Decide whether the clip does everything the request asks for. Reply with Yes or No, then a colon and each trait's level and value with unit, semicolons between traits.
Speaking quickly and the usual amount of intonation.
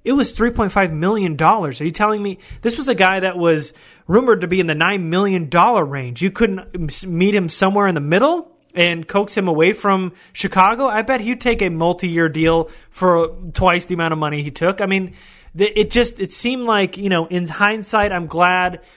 Yes: fast, 210 wpm; average, 3.7 semitones